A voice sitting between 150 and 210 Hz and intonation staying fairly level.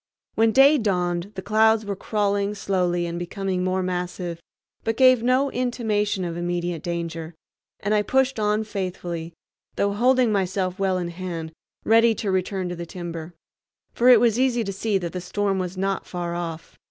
No: high, 190 Hz; average, 3.7 semitones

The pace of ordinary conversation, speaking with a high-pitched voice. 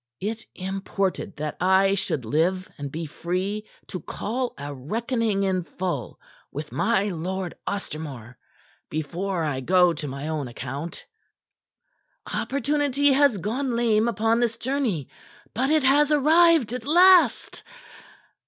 No: slow, 125 wpm; high, 195 Hz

